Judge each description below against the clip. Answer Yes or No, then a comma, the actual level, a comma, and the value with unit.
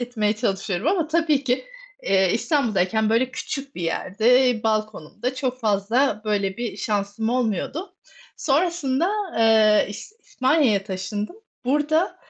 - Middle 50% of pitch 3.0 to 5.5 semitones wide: Yes, average, 4.9 semitones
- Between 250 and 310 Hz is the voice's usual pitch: No, high, 230 Hz